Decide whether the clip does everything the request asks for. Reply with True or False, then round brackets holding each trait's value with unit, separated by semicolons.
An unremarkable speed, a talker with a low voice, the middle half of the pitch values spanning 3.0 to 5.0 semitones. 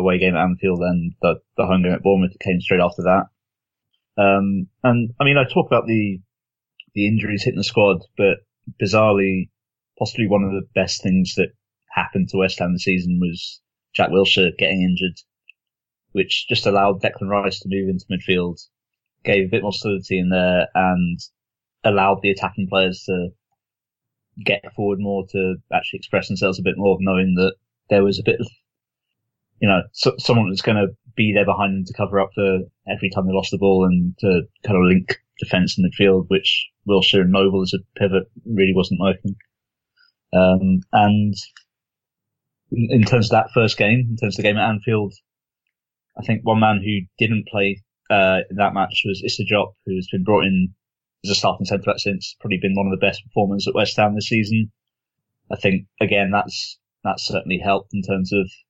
False (190 wpm; 100 Hz; 2.4 semitones)